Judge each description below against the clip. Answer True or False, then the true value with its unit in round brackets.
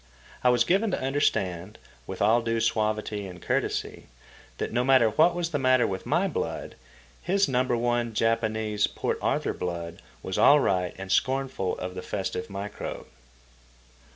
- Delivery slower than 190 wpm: True (155 wpm)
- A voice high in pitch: False (115 Hz)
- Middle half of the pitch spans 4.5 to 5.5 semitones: True (5.1 semitones)